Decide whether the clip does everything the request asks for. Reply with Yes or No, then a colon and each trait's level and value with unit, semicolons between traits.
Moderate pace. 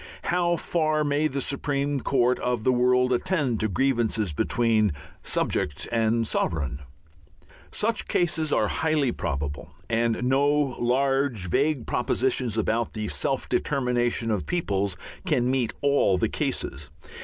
No: slow, 130 wpm